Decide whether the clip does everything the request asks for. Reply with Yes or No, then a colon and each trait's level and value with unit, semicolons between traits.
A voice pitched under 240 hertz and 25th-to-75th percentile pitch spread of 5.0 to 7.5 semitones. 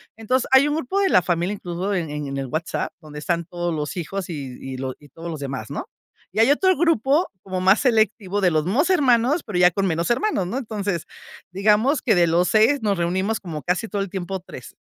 Yes: high, 190 Hz; wide, 5.4 semitones